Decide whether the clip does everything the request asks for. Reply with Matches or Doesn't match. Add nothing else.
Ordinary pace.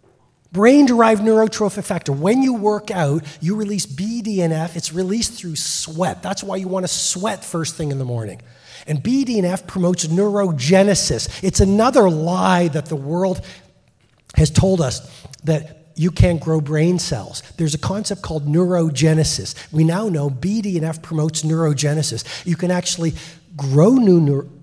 Matches